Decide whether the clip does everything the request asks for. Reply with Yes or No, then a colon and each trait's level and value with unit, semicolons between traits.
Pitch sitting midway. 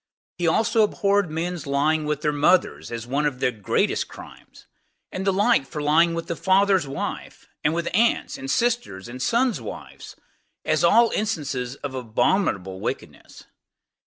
Yes: medium, 160 Hz